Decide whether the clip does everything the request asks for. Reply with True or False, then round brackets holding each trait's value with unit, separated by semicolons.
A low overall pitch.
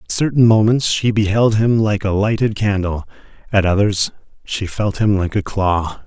True (105 Hz)